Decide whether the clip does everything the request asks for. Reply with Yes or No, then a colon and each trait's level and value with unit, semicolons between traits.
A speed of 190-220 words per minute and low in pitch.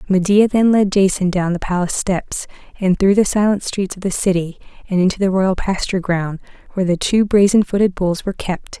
No: fast, 205 wpm; high, 190 Hz